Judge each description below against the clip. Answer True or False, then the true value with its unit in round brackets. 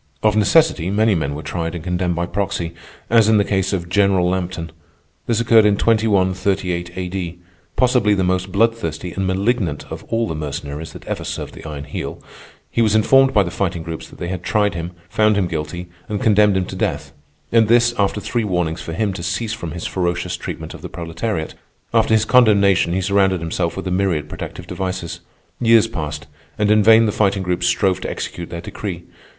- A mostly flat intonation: False (3.7 semitones)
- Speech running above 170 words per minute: True (200 wpm)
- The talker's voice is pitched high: False (95 Hz)